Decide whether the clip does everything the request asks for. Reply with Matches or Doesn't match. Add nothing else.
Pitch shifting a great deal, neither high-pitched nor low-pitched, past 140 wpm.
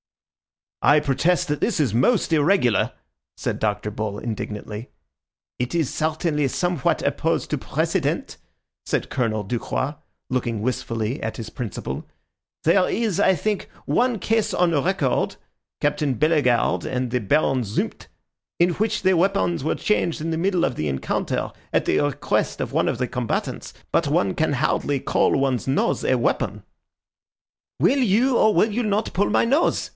Matches